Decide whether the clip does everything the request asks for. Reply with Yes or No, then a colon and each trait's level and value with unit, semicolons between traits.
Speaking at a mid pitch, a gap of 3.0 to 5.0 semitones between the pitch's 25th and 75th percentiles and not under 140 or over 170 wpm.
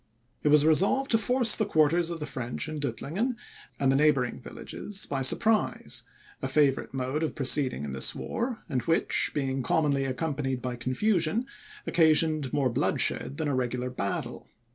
Yes: medium, 145 Hz; average, 4.1 semitones; average, 165 wpm